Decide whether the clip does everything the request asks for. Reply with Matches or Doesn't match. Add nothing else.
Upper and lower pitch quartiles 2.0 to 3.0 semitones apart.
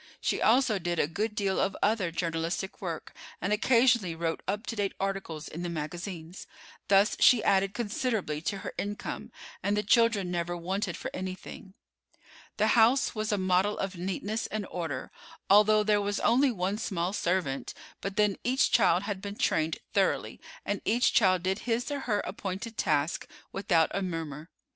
Doesn't match